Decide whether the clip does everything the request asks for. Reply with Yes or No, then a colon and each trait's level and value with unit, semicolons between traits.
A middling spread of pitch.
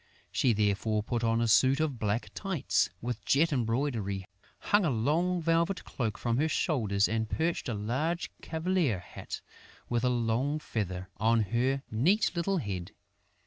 No: wide, 6.4 semitones